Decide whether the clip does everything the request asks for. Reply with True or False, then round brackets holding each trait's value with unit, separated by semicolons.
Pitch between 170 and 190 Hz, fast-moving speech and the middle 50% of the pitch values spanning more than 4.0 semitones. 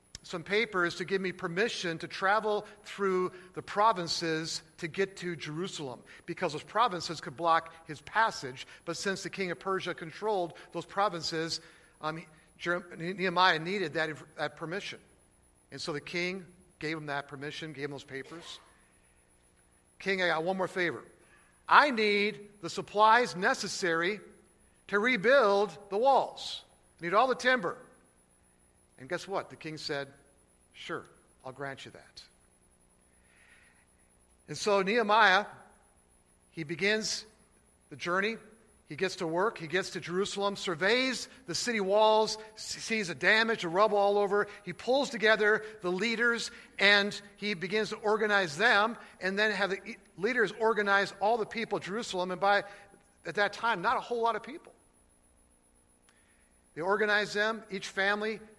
False (185 Hz; 145 wpm; 5.0 semitones)